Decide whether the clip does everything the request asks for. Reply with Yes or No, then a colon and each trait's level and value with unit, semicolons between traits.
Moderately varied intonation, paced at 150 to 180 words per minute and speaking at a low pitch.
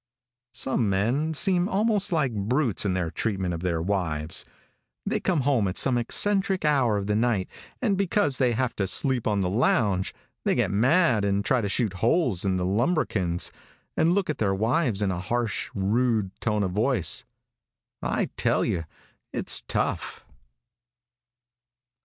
No: wide, 6.4 semitones; average, 160 wpm; low, 110 Hz